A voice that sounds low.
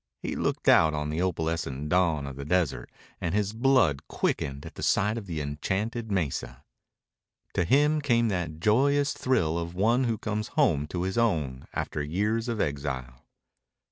Yes: very low, 90 Hz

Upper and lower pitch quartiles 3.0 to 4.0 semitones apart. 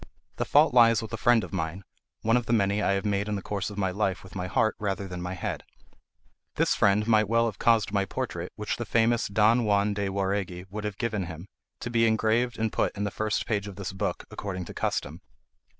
No: narrow, 2.6 semitones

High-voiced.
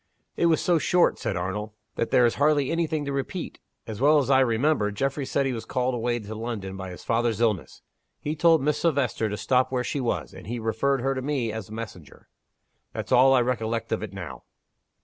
No: low, 120 Hz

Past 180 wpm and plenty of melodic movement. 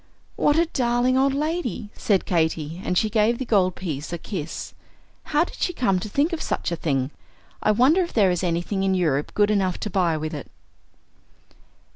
Yes: average, 195 wpm; wide, 6.7 semitones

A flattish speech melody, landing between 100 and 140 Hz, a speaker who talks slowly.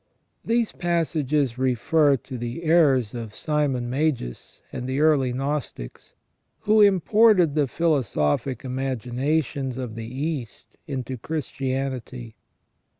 No: average, 4.0 semitones; low, 135 Hz; slow, 105 wpm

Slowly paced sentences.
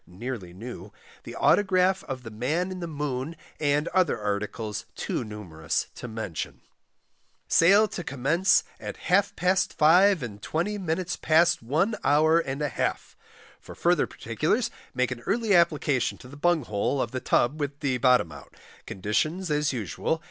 No: average, 160 wpm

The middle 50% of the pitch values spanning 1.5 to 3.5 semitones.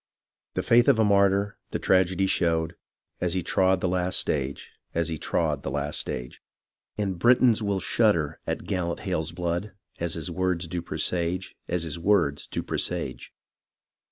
Yes: average, 2.8 semitones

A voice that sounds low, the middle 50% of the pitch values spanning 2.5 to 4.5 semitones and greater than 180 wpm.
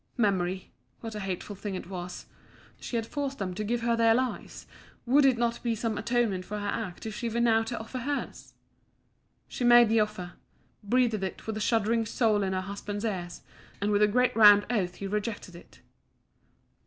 No: high, 215 Hz; average, 2.9 semitones; average, 195 wpm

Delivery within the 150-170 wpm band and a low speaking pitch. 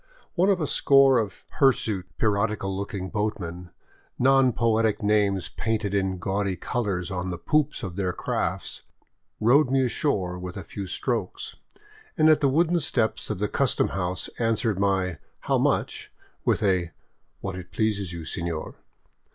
Yes: average, 165 wpm; low, 100 Hz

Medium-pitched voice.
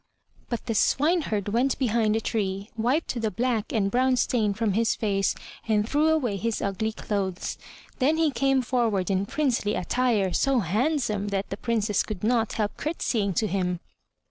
No: high, 220 Hz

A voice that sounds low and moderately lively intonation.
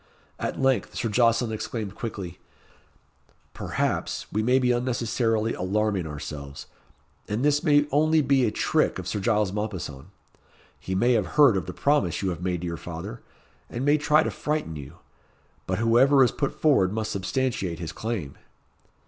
No: low, 110 Hz; wide, 6.0 semitones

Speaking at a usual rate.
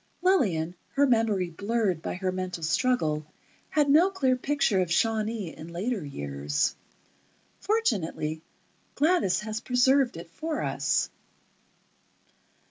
No: slow, 115 wpm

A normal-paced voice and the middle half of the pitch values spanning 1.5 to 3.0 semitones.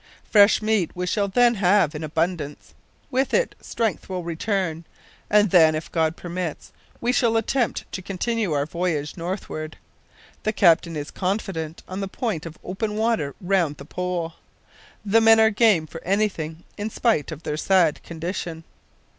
No: average, 160 wpm; average, 4.6 semitones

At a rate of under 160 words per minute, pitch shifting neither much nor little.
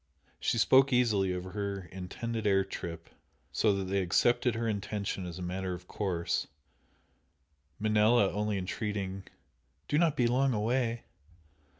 Yes: slow, 135 wpm; average, 3.7 semitones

